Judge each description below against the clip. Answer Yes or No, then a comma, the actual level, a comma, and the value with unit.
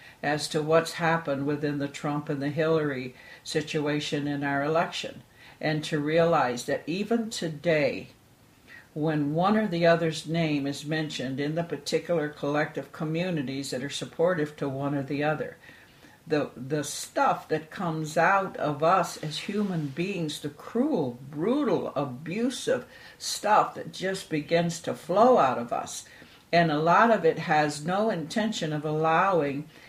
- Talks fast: No, average, 150 wpm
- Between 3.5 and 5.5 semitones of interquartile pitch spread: No, narrow, 2.4 semitones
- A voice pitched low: No, medium, 155 Hz